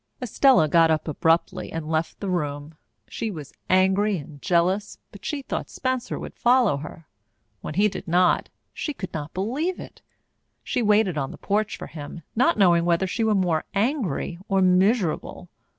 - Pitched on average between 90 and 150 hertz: No, medium, 185 Hz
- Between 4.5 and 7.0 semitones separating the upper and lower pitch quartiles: Yes, average, 4.8 semitones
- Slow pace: No, average, 170 wpm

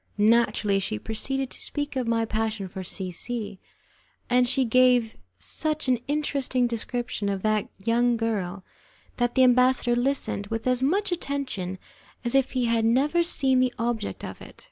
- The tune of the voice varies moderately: Yes, average, 3.2 semitones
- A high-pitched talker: Yes, high, 240 Hz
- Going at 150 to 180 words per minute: Yes, average, 165 wpm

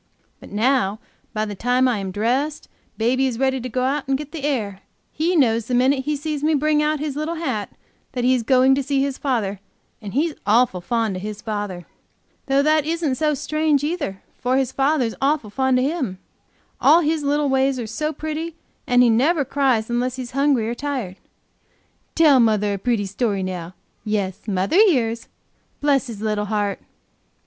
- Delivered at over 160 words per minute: Yes, average, 190 wpm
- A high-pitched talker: Yes, very high, 255 Hz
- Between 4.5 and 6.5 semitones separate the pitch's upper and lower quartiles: Yes, average, 5.1 semitones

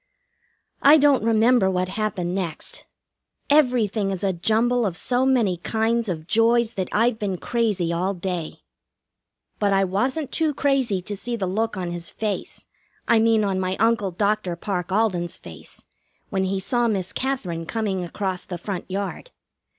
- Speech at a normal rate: Yes, average, 160 wpm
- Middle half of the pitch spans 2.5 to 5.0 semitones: Yes, average, 3.9 semitones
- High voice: Yes, high, 205 Hz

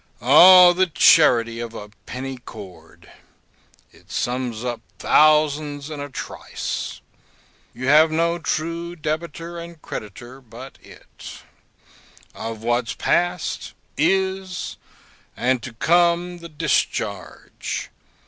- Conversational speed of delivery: No, slow, 105 wpm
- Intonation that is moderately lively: No, wide, 5.9 semitones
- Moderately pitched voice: Yes, medium, 150 Hz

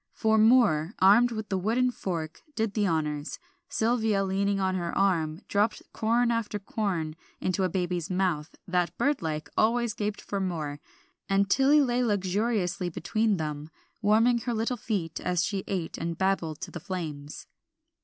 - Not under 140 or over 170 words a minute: Yes, average, 160 wpm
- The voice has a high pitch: Yes, high, 195 Hz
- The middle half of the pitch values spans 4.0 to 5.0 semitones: Yes, average, 4.5 semitones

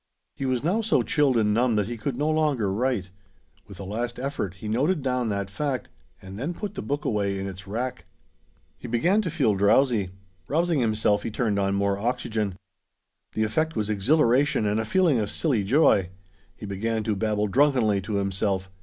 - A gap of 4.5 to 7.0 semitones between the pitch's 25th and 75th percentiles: Yes, wide, 5.5 semitones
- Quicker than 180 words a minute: Yes, average, 190 wpm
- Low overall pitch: Yes, low, 110 Hz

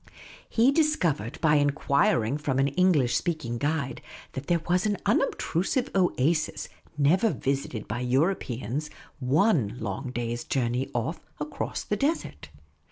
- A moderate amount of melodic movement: No, wide, 6.1 semitones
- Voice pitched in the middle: Yes, medium, 145 Hz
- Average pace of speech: No, slow, 130 wpm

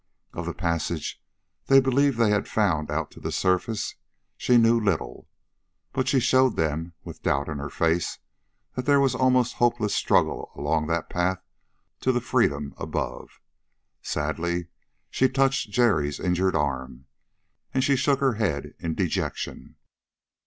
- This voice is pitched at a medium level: No, low, 100 Hz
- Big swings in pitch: Yes, wide, 8.0 semitones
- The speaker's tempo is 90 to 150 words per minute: Yes, average, 145 wpm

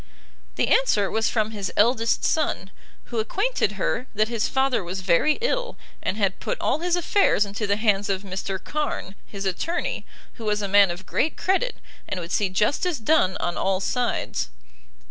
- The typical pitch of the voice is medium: No, high, 215 Hz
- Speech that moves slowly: No, average, 180 wpm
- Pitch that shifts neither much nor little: No, wide, 7.5 semitones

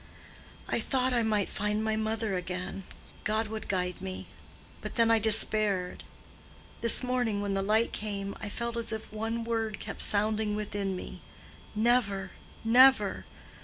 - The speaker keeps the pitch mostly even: Yes, narrow, 2.2 semitones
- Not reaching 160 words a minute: Yes, average, 140 wpm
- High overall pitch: Yes, high, 215 Hz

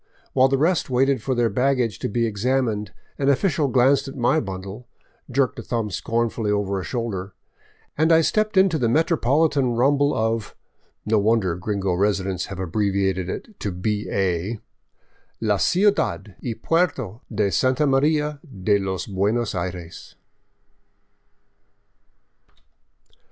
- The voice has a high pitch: No, low, 115 Hz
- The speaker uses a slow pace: No, average, 145 wpm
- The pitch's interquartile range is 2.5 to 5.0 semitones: No, wide, 5.6 semitones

